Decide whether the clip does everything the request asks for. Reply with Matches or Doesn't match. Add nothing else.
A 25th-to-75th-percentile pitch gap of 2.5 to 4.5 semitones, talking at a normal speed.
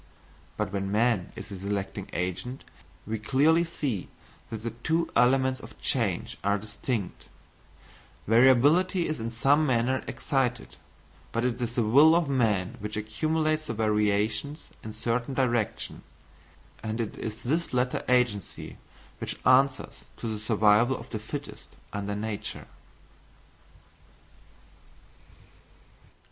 Doesn't match